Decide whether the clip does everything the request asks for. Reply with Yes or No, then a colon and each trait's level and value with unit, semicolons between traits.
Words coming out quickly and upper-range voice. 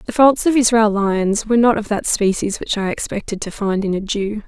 Yes: fast, 240 wpm; high, 215 Hz